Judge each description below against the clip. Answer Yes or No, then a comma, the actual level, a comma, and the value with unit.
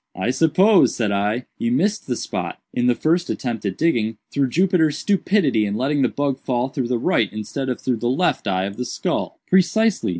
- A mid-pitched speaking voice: No, low, 130 Hz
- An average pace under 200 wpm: No, fast, 205 wpm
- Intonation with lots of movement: Yes, wide, 6.0 semitones